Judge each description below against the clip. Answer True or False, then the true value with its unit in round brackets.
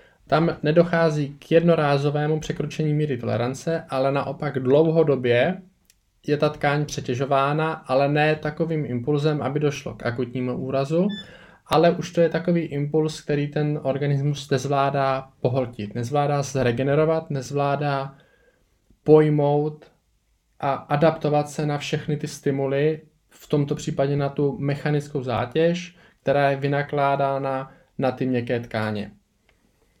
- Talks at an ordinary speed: False (120 wpm)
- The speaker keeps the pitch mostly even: True (2.3 semitones)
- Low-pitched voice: False (145 Hz)